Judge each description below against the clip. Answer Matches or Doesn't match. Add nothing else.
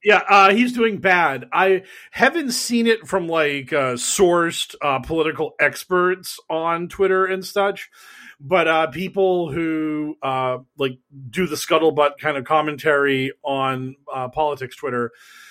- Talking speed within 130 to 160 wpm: Matches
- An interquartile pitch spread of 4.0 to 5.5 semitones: Matches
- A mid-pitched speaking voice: Matches